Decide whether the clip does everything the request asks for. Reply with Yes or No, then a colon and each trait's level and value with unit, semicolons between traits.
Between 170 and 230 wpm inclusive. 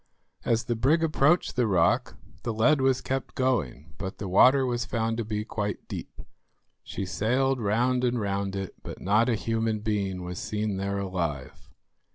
Yes: average, 175 wpm